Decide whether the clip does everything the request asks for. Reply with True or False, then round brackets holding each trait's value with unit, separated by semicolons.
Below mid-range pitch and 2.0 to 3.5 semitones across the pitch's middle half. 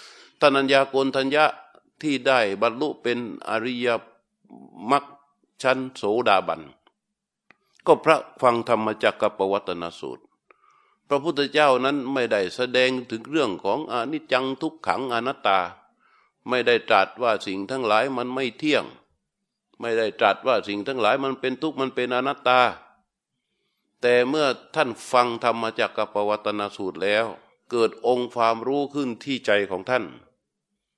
True (125 Hz; 3.2 semitones)